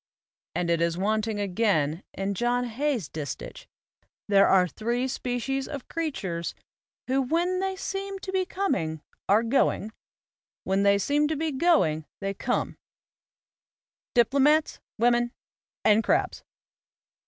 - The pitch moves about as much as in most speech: No, wide, 7.1 semitones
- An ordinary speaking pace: No, slow, 125 wpm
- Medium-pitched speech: No, high, 240 Hz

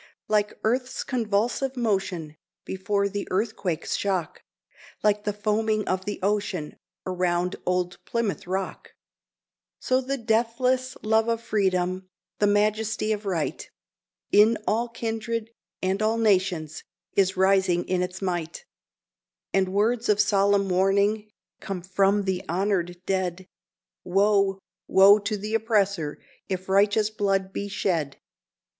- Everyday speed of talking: No, slow, 125 wpm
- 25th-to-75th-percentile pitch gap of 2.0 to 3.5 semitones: Yes, narrow, 2.5 semitones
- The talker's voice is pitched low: No, high, 200 Hz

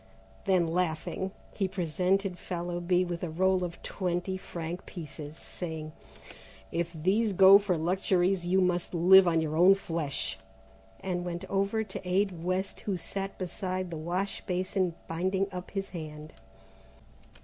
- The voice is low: No, medium, 180 Hz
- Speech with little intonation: Yes, narrow, 2.0 semitones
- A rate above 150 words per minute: No, average, 140 wpm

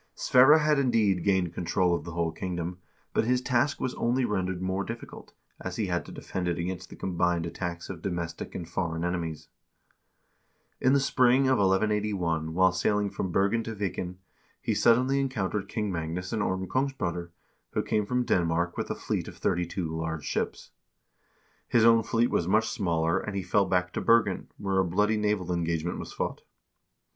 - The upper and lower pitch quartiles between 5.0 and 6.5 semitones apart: No, average, 4.3 semitones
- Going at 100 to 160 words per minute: No, average, 180 wpm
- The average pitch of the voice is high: No, very low, 95 Hz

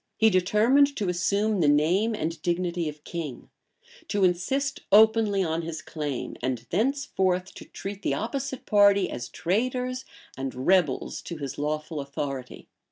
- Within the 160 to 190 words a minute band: No, average, 145 wpm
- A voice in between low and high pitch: Yes, medium, 180 Hz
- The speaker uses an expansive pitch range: Yes, wide, 6.1 semitones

